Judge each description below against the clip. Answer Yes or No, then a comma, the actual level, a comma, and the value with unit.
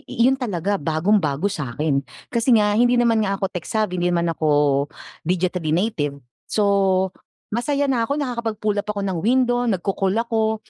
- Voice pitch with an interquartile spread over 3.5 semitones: Yes, average, 5.0 semitones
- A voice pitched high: Yes, high, 200 Hz